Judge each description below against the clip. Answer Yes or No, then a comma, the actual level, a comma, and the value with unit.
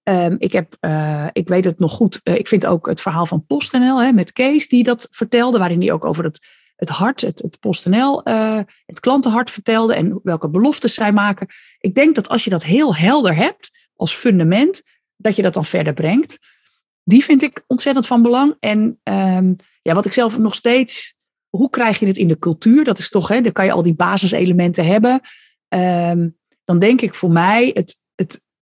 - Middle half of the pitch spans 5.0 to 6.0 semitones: Yes, average, 5.3 semitones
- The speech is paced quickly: Yes, fast, 205 wpm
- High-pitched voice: Yes, high, 210 Hz